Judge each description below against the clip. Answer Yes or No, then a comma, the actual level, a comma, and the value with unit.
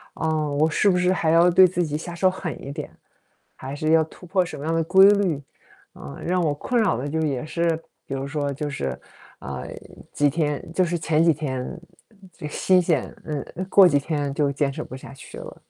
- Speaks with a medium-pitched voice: Yes, medium, 155 Hz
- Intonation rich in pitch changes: No, average, 3.7 semitones